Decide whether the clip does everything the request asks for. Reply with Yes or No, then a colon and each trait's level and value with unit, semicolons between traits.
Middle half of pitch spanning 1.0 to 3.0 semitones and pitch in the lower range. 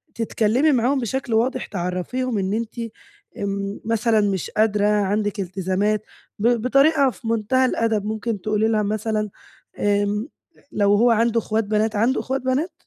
No: narrow, 2.6 semitones; high, 220 Hz